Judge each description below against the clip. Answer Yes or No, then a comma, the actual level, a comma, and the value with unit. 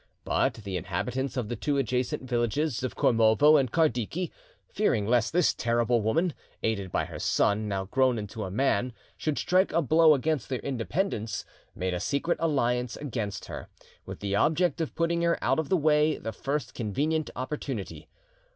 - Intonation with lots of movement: Yes, wide, 5.7 semitones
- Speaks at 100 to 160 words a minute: No, average, 170 wpm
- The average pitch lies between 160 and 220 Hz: No, low, 130 Hz